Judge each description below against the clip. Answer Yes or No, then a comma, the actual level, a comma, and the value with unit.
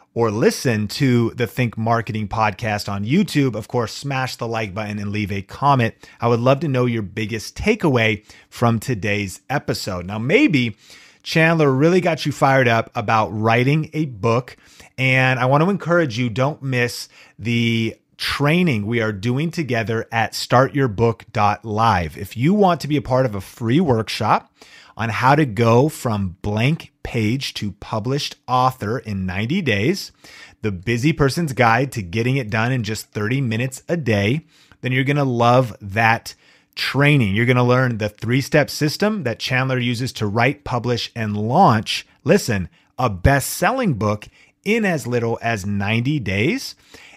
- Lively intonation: No, average, 4.0 semitones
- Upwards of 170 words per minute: No, average, 165 wpm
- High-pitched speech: No, low, 120 Hz